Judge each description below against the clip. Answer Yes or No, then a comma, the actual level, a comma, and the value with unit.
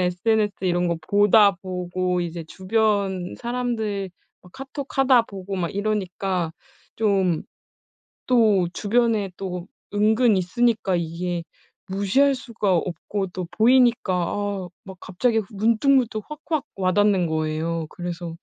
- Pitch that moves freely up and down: No, average, 3.8 semitones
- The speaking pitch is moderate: No, high, 195 Hz